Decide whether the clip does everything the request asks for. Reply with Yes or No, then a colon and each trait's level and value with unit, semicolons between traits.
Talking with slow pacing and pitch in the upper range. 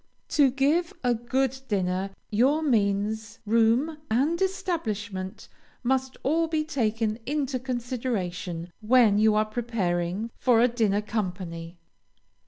Yes: slow, 115 wpm; high, 230 Hz